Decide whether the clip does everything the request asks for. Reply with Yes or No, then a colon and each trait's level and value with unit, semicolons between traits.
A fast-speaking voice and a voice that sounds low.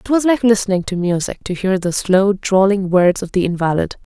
No: fast, 215 wpm; high, 195 Hz